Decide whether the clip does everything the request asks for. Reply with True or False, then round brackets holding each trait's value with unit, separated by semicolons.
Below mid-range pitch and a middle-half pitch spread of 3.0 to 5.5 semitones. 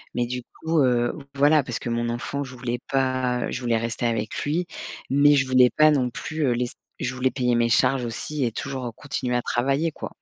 False (125 Hz; 2.5 semitones)